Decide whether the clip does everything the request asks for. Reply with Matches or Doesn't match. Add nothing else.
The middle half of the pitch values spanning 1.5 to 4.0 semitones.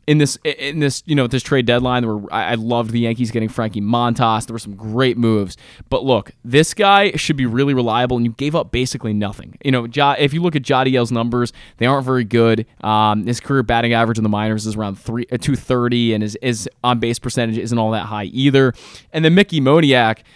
Matches